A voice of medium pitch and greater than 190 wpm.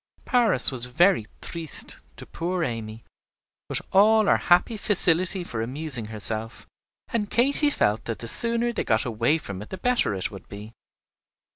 No: medium, 155 Hz; average, 160 wpm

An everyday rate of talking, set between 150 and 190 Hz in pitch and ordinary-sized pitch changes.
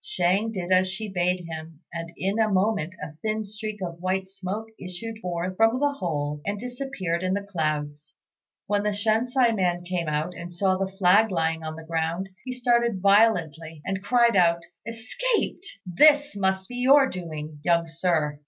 Yes: average, 175 wpm; medium, 185 Hz; average, 4.5 semitones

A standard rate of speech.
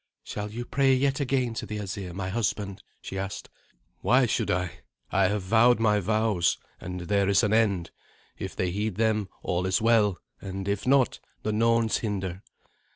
Yes: average, 175 wpm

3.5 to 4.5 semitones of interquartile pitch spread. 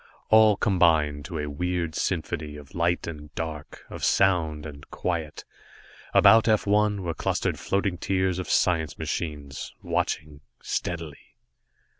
Yes: average, 3.8 semitones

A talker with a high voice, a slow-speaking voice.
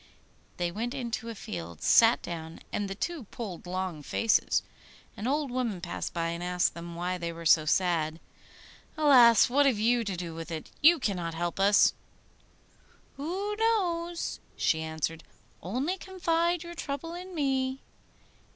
No: high, 215 Hz; average, 155 wpm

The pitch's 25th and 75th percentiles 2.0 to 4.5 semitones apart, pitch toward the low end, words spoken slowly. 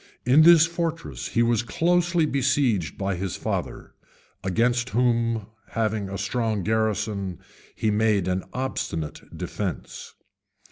No: average, 4.9 semitones; low, 115 Hz; slow, 120 wpm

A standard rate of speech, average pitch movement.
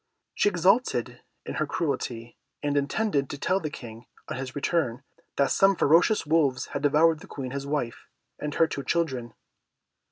Yes: average, 165 wpm; average, 4.3 semitones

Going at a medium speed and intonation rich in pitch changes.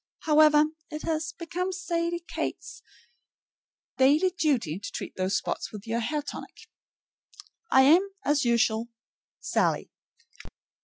No: slow, 115 wpm; wide, 6.1 semitones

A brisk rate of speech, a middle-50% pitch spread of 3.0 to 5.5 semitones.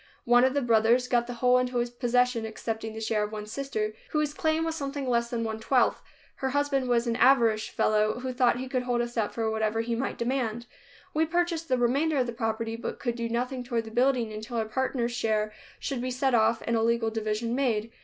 No: fast, 225 wpm; narrow, 2.5 semitones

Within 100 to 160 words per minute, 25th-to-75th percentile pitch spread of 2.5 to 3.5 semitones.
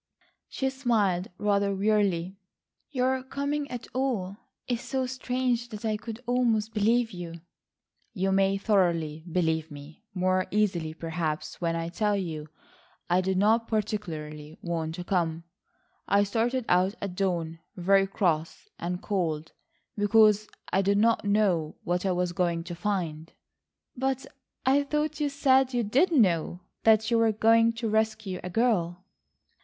No: average, 145 wpm; average, 4.7 semitones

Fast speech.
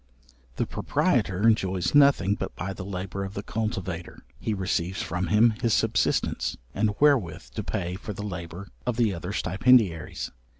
No: average, 160 wpm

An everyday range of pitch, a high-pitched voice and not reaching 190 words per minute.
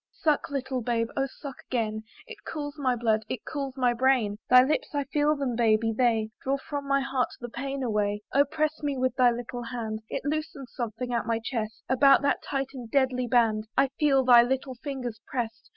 No: average, 3.0 semitones; very high, 255 Hz; average, 200 wpm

